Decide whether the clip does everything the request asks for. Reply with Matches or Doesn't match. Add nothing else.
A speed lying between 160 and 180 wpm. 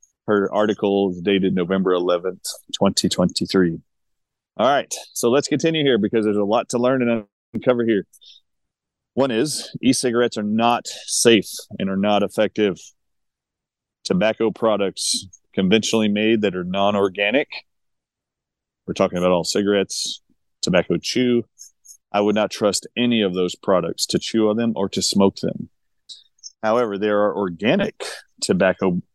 Doesn't match